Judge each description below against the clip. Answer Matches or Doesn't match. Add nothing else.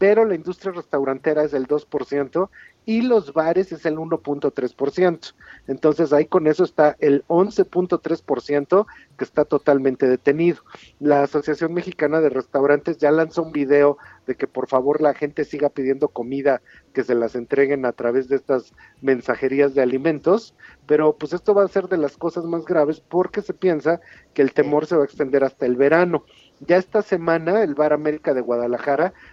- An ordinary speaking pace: Matches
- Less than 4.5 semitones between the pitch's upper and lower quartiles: Matches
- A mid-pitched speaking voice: Matches